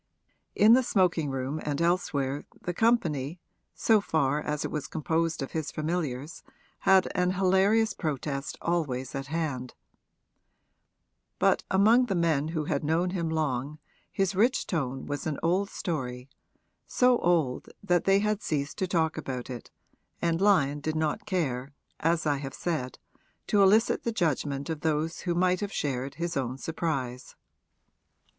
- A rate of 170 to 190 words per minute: No, average, 150 wpm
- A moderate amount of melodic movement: Yes, average, 4.5 semitones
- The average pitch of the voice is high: No, medium, 160 Hz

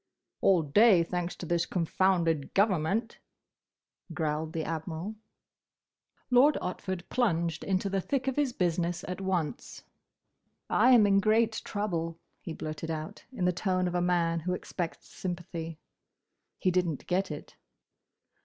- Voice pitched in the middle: Yes, medium, 180 Hz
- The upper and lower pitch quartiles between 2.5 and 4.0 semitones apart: Yes, average, 3.1 semitones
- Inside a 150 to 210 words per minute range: No, slow, 135 wpm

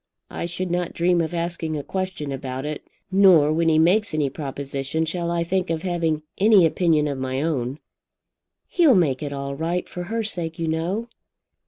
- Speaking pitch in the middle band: Yes, medium, 165 Hz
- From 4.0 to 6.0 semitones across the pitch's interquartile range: No, average, 3.2 semitones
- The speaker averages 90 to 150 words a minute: No, average, 185 wpm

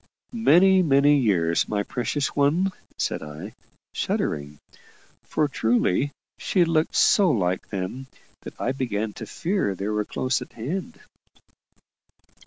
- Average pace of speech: No, slow, 125 wpm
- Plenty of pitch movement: Yes, wide, 7.4 semitones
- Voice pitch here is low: Yes, low, 130 Hz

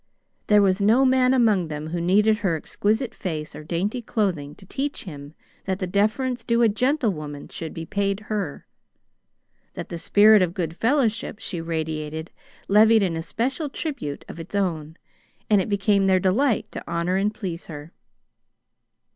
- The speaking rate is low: No, average, 165 wpm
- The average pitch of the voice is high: Yes, high, 195 Hz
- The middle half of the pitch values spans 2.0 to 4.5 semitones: No, average, 4.9 semitones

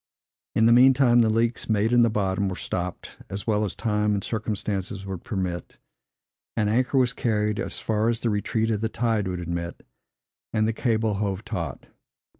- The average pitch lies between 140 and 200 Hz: No, low, 110 Hz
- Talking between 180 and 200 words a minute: Yes, average, 190 wpm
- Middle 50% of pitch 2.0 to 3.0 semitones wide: Yes, narrow, 2.6 semitones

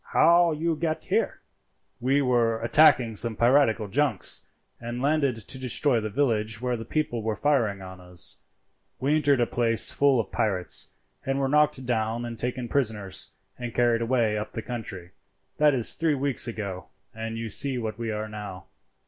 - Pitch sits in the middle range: No, low, 120 Hz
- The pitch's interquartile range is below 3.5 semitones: No, average, 4.0 semitones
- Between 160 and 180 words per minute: Yes, average, 175 wpm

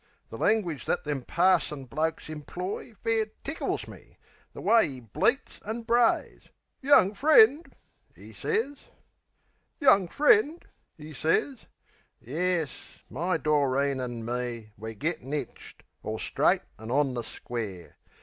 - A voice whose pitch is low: No, medium, 155 Hz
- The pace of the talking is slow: Yes, slow, 120 wpm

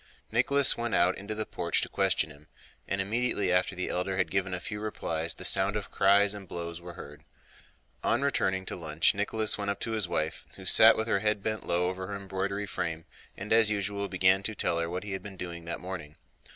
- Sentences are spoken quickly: Yes, fast, 225 wpm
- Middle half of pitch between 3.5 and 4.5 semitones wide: No, average, 2.7 semitones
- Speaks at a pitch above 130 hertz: No, very low, 95 Hz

